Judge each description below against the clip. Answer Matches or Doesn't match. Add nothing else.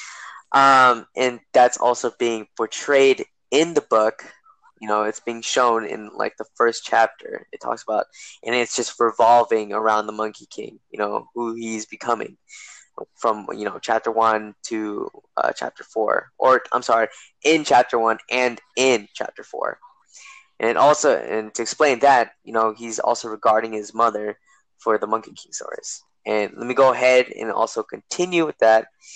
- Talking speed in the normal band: Matches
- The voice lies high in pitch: Doesn't match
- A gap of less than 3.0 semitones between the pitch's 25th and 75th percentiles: Matches